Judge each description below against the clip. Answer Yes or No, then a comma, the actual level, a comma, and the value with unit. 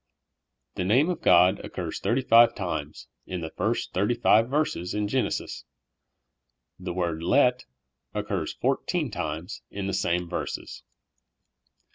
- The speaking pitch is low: Yes, low, 100 Hz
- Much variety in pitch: Yes, wide, 6.1 semitones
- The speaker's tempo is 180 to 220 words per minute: No, average, 140 wpm